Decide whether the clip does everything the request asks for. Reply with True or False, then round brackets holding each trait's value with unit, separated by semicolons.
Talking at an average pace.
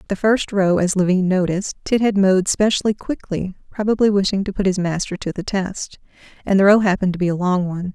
False (220 wpm)